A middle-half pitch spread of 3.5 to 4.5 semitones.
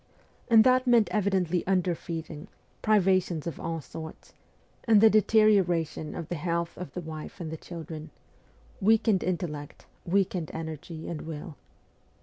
Yes: average, 3.8 semitones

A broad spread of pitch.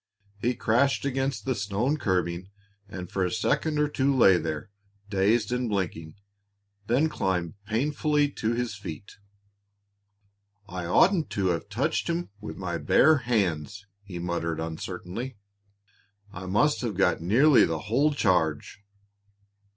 Yes: wide, 6.7 semitones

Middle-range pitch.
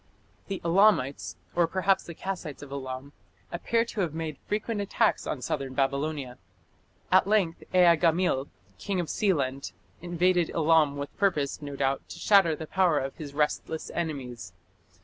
Yes: medium, 160 Hz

